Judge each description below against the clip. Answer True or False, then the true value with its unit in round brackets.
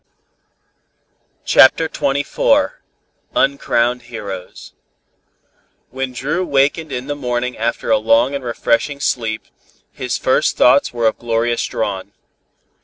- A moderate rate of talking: False (110 wpm)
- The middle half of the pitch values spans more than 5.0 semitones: False (3.4 semitones)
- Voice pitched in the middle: False (125 Hz)